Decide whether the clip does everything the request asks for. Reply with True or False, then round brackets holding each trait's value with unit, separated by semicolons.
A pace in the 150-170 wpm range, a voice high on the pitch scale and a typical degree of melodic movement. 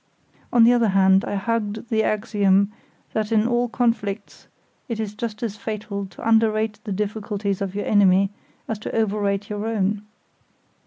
False (160 wpm; 210 Hz; 2.0 semitones)